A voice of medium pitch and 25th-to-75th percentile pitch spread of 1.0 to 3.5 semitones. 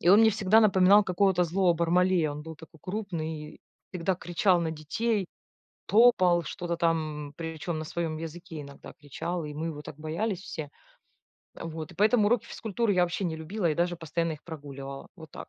Yes: medium, 170 Hz; average, 3.2 semitones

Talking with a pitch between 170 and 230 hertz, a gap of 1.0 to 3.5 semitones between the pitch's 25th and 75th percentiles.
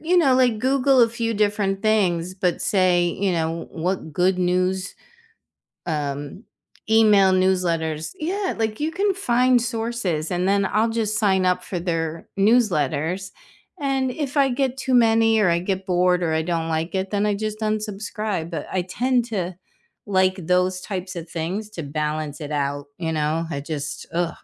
No: high, 190 Hz; average, 4.8 semitones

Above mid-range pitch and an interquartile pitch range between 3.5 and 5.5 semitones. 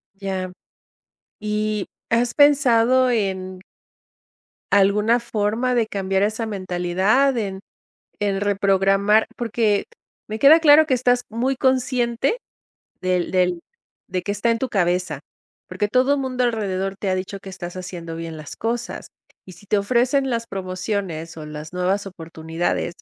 Yes: high, 205 Hz; average, 4.3 semitones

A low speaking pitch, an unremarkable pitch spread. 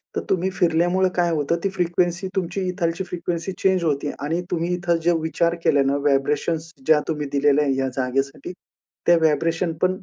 No: medium, 165 Hz; average, 3.0 semitones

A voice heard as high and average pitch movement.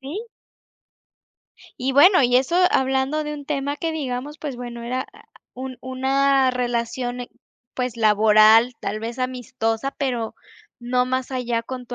No: very high, 255 Hz; narrow, 2.1 semitones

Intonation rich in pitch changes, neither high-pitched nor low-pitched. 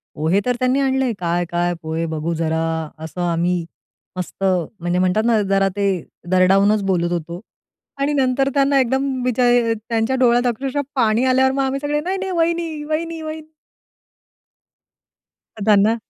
No: wide, 7.2 semitones; high, 235 Hz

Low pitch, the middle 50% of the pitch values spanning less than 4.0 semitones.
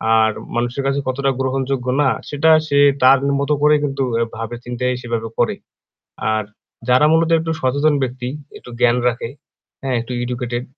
Yes: low, 130 Hz; narrow, 2.5 semitones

